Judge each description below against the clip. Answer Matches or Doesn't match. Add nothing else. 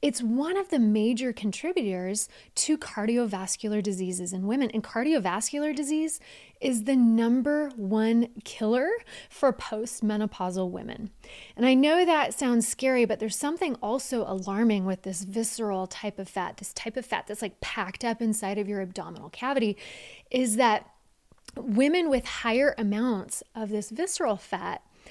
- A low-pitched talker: Doesn't match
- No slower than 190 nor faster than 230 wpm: Doesn't match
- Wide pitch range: Doesn't match